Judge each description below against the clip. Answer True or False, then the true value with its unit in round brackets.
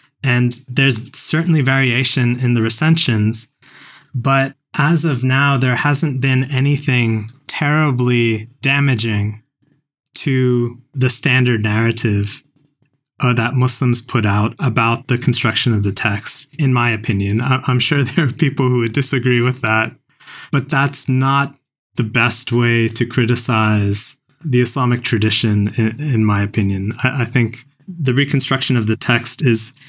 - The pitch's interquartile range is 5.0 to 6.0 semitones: False (3.1 semitones)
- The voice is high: False (125 Hz)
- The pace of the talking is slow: True (130 wpm)